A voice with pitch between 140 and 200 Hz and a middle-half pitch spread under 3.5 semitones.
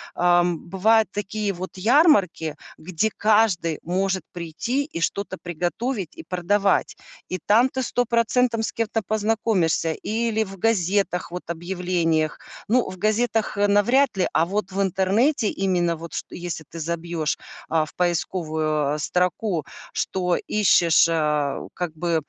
No: medium, 185 Hz; average, 4.3 semitones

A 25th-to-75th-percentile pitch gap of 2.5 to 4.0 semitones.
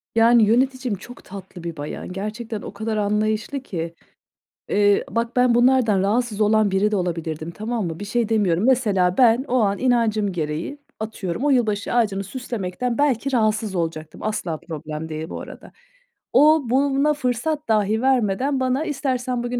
No: average, 4.5 semitones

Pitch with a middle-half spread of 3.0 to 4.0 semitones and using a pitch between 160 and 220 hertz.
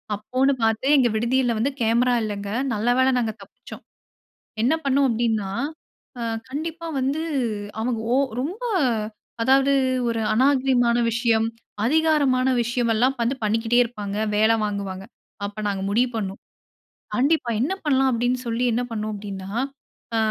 No: average, 3.4 semitones; high, 235 Hz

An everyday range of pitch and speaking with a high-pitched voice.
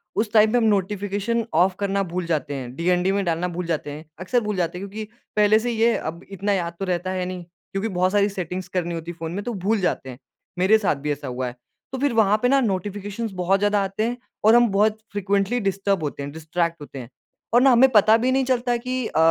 Yes: average, 3.9 semitones; high, 195 Hz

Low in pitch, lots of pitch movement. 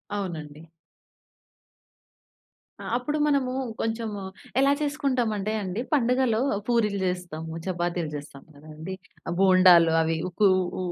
No: high, 190 Hz; wide, 6.2 semitones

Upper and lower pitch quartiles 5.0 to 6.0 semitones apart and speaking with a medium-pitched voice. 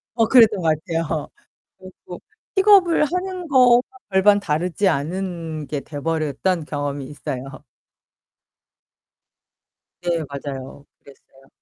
No: wide, 6.4 semitones; medium, 165 Hz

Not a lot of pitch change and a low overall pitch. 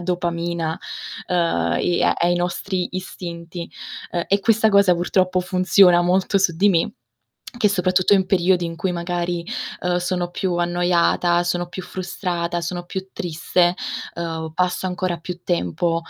No: narrow, 1.2 semitones; medium, 175 Hz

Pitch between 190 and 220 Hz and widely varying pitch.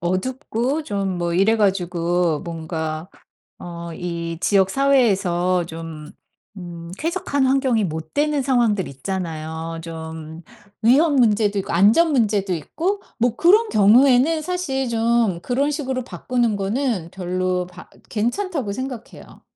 Yes: high, 200 Hz; wide, 7.2 semitones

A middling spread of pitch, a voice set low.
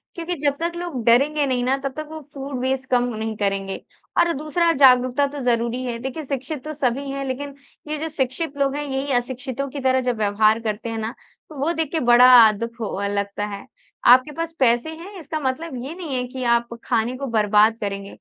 No: average, 3.8 semitones; very high, 260 Hz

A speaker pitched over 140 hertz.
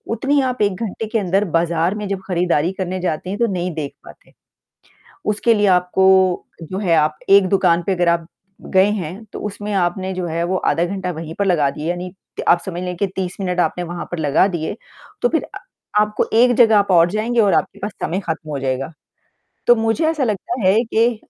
Yes: medium, 185 Hz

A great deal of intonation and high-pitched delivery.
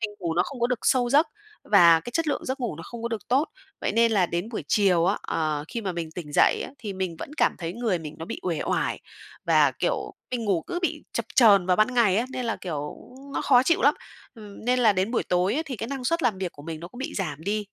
Yes: wide, 5.9 semitones; high, 210 Hz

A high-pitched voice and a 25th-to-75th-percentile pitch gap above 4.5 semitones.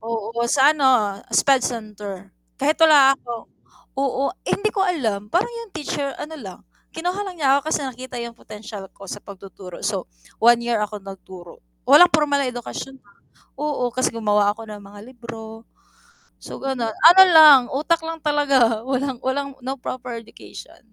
Yes: very high, 255 Hz; average, 5.0 semitones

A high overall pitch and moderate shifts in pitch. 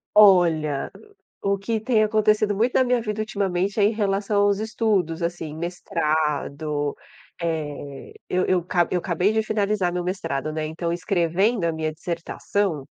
No: medium, 180 Hz; average, 4.5 semitones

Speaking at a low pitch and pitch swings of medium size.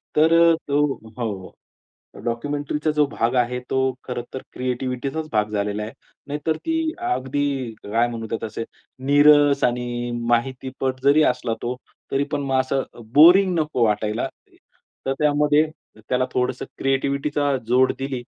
Yes: low, 130 Hz; average, 3.3 semitones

